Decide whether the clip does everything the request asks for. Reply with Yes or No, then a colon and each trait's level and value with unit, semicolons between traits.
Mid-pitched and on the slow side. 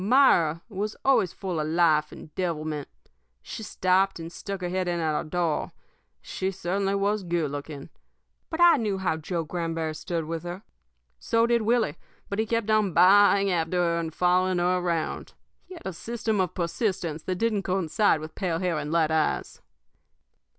No: medium, 180 Hz; average, 185 wpm